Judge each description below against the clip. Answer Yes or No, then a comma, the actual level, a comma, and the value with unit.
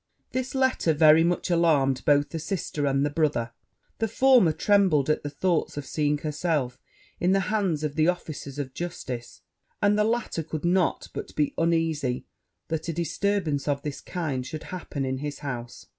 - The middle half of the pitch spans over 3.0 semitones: Yes, average, 3.7 semitones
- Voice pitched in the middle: Yes, medium, 155 Hz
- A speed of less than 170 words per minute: No, average, 175 wpm